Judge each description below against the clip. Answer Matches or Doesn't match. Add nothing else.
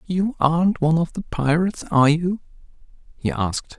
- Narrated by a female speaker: Doesn't match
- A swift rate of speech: Doesn't match